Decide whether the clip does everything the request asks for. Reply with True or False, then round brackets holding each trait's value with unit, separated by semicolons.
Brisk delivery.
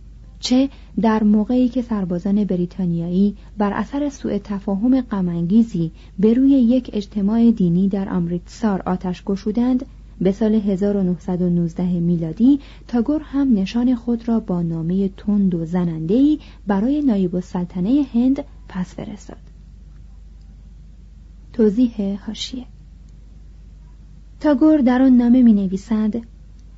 False (110 wpm)